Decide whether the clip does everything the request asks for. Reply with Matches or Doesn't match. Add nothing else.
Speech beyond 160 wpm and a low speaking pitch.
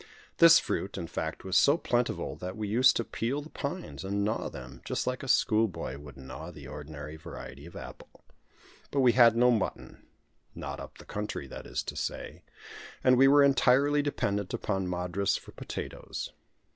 Matches